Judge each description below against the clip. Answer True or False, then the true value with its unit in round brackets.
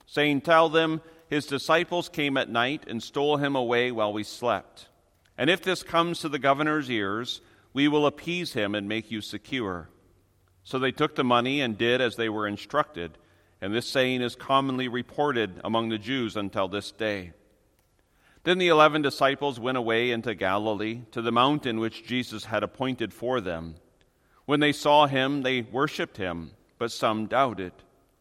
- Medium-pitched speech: False (120 Hz)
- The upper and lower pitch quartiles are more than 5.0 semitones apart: True (5.6 semitones)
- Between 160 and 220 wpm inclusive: True (170 wpm)